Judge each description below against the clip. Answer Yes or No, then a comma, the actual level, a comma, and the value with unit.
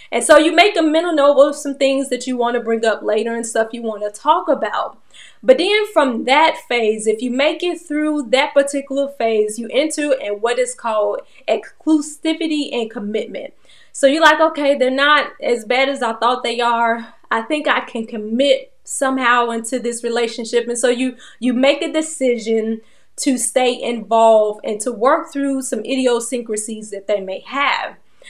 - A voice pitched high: Yes, very high, 255 Hz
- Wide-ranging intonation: No, average, 4.0 semitones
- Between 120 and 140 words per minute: No, average, 185 wpm